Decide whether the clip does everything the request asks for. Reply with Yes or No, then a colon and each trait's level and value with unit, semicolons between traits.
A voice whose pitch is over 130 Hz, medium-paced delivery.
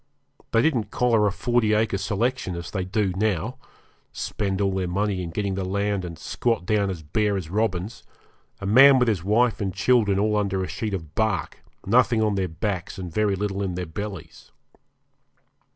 No: low, 100 Hz; average, 185 wpm